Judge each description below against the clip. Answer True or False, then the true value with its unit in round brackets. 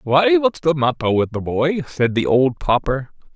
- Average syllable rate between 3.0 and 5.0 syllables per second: True (4.6 syllables/s)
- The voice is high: False (140 Hz)